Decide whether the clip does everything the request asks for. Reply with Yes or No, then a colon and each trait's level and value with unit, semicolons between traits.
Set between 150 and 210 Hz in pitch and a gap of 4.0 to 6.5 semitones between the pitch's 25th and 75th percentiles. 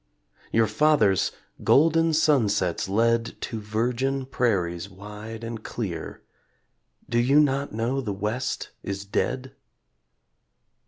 No: low, 115 Hz; average, 4.4 semitones